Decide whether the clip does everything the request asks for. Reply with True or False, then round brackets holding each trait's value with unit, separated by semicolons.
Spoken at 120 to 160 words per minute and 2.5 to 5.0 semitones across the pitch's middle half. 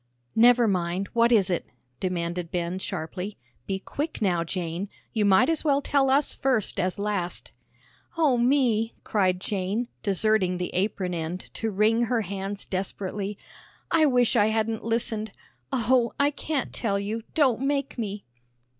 True (150 wpm; 4.5 semitones)